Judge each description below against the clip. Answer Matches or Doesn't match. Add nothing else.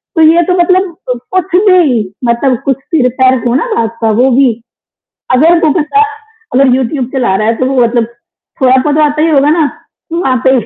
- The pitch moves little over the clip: Doesn't match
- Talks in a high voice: Matches